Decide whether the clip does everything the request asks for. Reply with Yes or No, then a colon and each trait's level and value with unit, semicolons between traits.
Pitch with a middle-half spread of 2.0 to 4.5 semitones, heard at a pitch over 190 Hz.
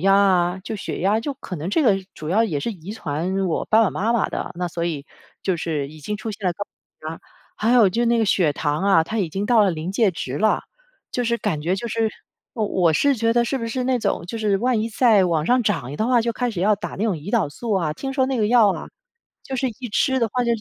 No: average, 4.9 semitones; high, 205 Hz